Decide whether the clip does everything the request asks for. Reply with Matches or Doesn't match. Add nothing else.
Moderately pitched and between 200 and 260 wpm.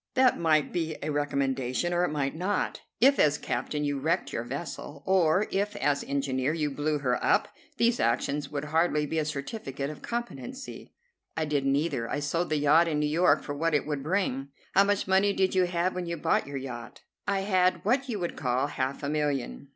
Matches